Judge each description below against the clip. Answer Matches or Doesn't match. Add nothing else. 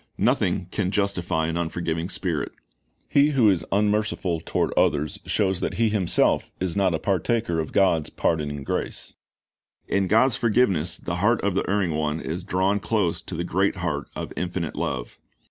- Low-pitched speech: Matches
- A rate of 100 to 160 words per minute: Doesn't match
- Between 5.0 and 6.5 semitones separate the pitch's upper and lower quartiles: Doesn't match